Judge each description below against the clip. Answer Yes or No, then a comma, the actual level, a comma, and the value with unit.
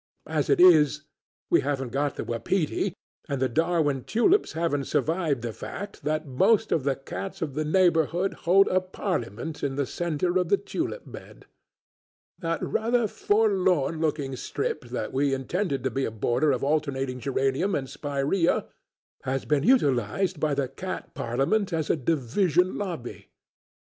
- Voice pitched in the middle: Yes, medium, 150 Hz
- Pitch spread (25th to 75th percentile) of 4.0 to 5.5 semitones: Yes, average, 5.2 semitones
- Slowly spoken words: No, average, 155 wpm